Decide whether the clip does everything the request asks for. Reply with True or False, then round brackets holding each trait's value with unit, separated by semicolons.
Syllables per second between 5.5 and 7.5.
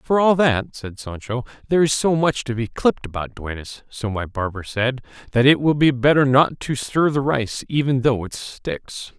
False (4.7 syllables/s)